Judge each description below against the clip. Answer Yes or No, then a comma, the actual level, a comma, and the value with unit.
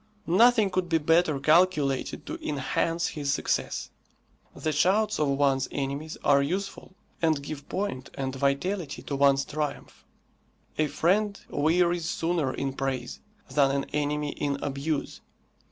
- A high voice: No, medium, 150 Hz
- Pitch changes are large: No, average, 4.0 semitones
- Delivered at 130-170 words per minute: Yes, slow, 135 wpm